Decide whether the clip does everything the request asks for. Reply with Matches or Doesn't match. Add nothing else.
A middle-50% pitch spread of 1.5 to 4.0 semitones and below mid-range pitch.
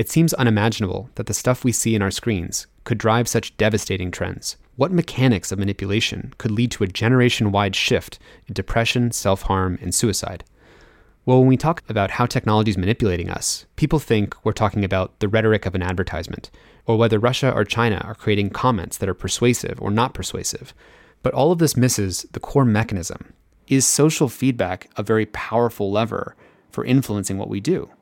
Matches